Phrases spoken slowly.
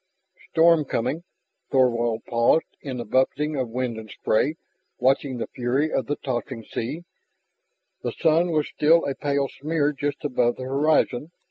No: average, 155 wpm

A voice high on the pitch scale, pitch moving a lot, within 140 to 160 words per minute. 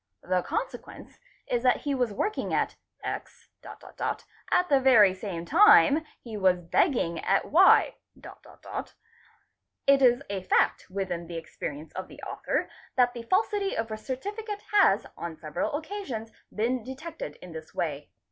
Yes: high, 235 Hz; wide, 8.6 semitones; average, 145 wpm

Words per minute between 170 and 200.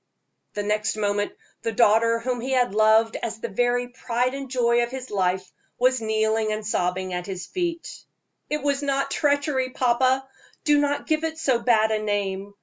Yes: average, 180 wpm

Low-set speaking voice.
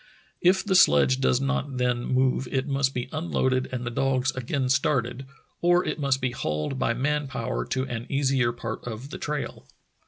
Yes: low, 130 Hz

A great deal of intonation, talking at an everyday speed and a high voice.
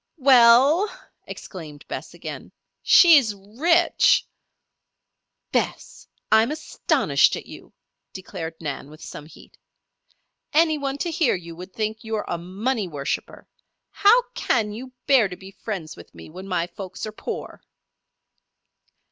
No: wide, 7.3 semitones; slow, 130 wpm; high, 215 Hz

